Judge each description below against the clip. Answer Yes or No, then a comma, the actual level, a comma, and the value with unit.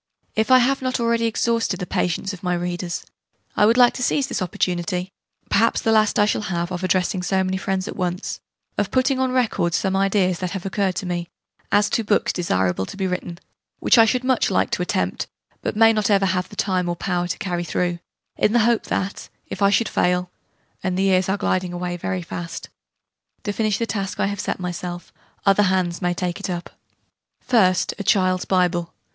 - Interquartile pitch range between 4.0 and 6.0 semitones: No, average, 3.1 semitones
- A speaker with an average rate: No, fast, 210 wpm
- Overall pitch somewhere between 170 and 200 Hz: Yes, high, 190 Hz